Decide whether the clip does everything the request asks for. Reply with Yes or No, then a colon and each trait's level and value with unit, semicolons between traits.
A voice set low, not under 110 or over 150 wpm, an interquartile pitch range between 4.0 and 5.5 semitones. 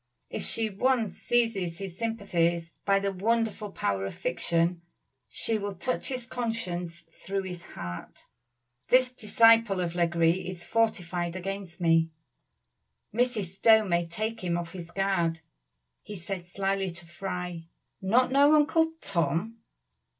No: high, 190 Hz; slow, 135 wpm; average, 4.7 semitones